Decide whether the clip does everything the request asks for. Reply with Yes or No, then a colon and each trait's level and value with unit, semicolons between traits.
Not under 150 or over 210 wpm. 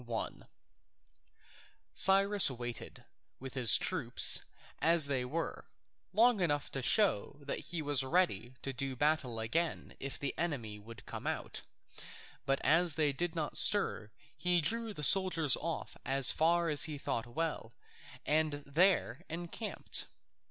No: average, 140 wpm